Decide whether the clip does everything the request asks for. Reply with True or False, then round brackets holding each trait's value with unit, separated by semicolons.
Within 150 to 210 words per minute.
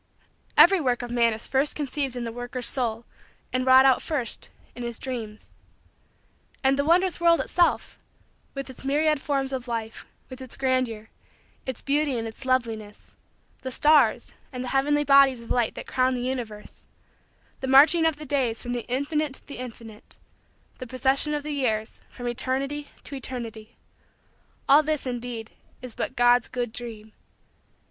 True (165 wpm)